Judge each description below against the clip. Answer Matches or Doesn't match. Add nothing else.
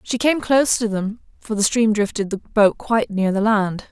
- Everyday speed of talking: Doesn't match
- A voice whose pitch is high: Matches